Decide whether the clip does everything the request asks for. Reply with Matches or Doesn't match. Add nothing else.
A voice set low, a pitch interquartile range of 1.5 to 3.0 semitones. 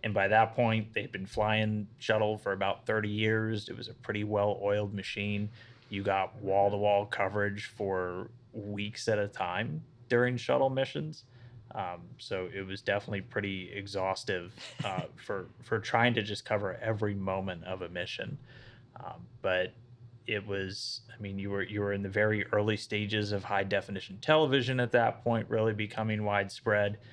Matches